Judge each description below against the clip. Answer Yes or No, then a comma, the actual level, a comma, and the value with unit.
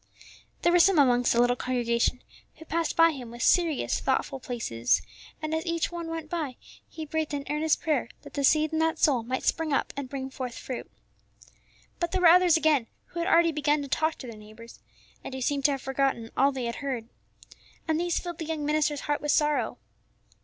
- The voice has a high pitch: Yes, very high, 295 Hz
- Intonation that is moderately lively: Yes, average, 4.1 semitones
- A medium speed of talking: No, fast, 210 wpm